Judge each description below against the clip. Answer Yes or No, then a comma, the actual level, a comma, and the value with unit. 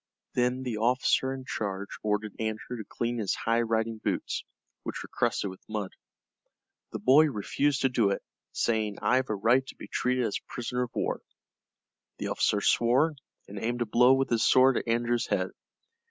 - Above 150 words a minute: Yes, average, 185 wpm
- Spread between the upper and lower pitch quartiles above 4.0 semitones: No, average, 2.8 semitones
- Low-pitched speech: Yes, low, 120 Hz